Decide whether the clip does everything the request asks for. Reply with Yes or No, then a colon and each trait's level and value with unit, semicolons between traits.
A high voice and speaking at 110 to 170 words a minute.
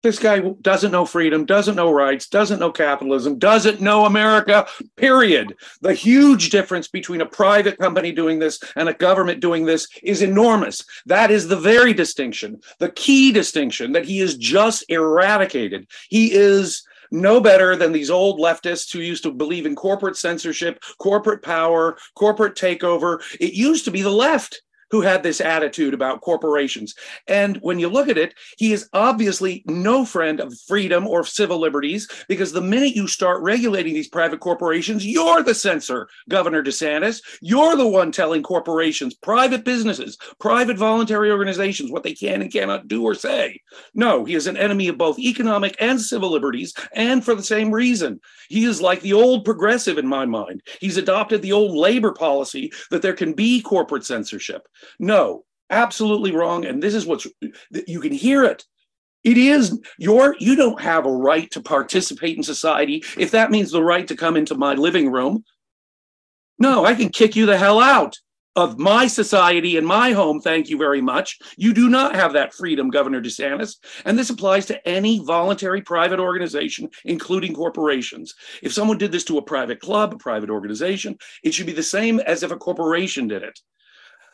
No: high, 195 Hz; average, 180 wpm